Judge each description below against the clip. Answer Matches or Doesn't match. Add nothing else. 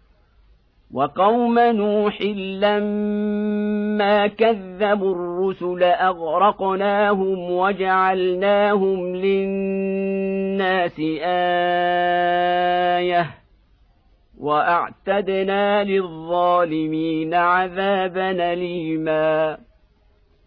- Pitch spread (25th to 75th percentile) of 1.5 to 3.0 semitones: Matches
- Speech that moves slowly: Matches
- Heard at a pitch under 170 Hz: Doesn't match